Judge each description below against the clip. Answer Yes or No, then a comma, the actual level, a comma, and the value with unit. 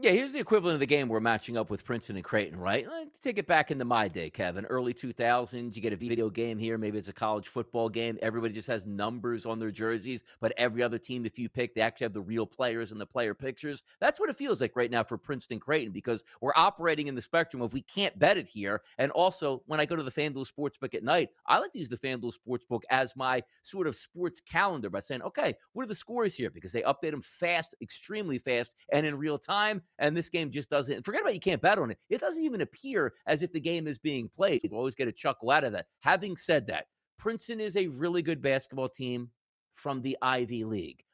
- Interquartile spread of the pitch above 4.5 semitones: Yes, average, 4.9 semitones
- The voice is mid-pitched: No, low, 130 Hz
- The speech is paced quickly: Yes, fast, 255 wpm